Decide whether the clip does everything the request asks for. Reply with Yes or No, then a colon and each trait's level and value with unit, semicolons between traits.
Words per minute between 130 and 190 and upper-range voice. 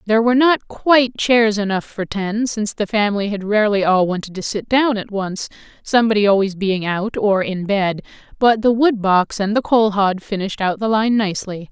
No: fast, 205 wpm; high, 210 Hz